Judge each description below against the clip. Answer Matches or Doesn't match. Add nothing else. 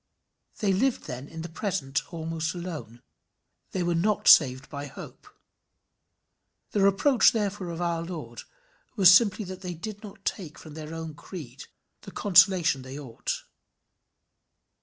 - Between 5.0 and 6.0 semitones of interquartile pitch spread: Doesn't match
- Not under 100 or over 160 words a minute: Matches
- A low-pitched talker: Doesn't match